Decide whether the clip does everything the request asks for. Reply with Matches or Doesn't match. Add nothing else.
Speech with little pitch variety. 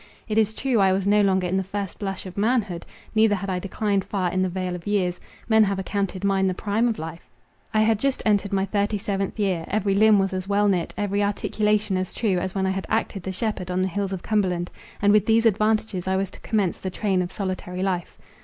Matches